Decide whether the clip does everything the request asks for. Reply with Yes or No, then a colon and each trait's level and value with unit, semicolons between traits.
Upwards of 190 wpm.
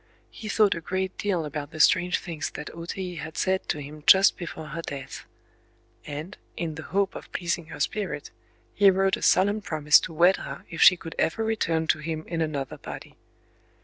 Yes: average, 200 wpm